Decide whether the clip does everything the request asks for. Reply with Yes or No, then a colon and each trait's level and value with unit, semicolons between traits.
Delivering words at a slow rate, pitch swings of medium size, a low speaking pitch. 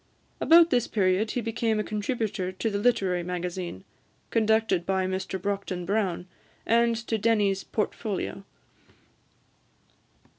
No: slow, 115 wpm; average, 3.2 semitones; high, 205 Hz